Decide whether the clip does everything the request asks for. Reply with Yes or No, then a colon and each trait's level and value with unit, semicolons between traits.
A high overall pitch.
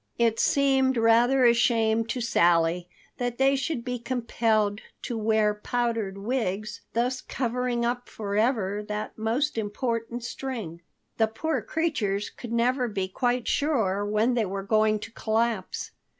Yes: high, 230 Hz